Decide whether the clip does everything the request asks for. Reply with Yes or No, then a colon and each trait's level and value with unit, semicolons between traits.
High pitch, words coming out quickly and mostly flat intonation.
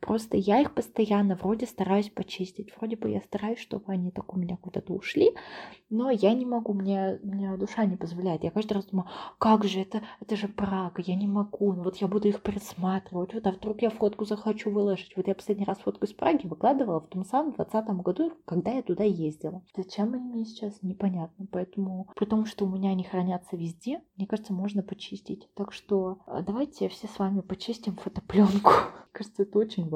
Yes: high, 200 Hz; fast, 200 wpm; narrow, 2.2 semitones